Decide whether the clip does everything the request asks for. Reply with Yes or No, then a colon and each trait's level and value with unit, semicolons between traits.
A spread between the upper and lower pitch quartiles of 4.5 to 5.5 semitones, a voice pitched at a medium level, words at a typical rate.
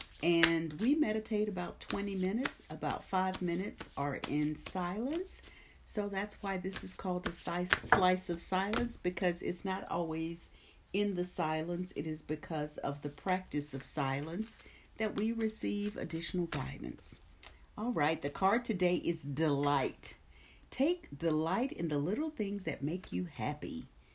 Yes: average, 4.8 semitones; medium, 180 Hz; average, 145 wpm